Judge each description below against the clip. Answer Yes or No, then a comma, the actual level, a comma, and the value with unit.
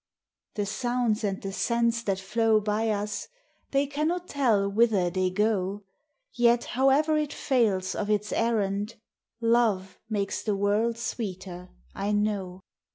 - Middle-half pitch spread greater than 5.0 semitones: No, average, 3.0 semitones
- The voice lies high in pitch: Yes, high, 215 Hz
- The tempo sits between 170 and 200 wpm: No, average, 140 wpm